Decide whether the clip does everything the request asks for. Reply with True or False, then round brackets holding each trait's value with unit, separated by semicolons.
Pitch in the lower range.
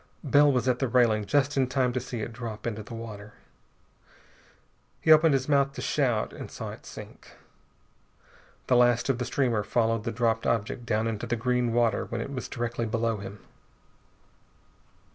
True (120 Hz)